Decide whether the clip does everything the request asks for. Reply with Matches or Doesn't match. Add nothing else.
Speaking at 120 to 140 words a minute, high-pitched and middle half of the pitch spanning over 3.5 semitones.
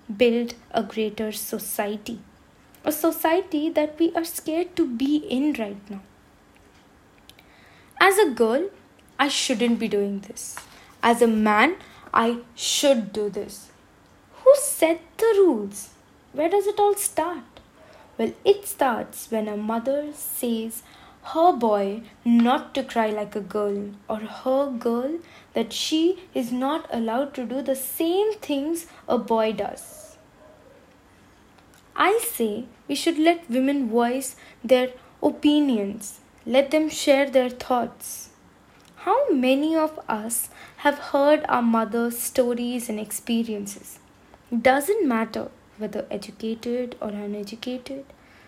Matches